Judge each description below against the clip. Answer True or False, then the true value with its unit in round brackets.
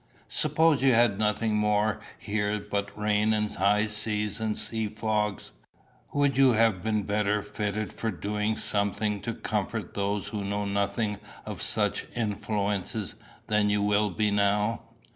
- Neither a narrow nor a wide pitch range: False (1.1 semitones)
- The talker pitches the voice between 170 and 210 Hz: False (105 Hz)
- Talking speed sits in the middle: True (145 wpm)